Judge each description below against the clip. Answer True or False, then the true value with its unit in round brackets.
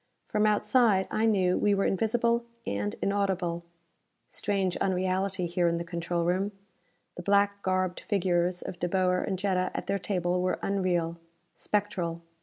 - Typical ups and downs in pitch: False (2.3 semitones)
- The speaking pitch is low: False (185 Hz)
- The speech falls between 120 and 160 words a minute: True (150 wpm)